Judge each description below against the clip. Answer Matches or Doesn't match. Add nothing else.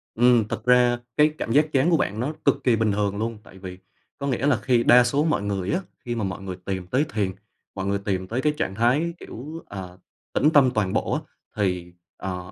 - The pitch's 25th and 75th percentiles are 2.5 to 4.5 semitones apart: Doesn't match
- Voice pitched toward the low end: Matches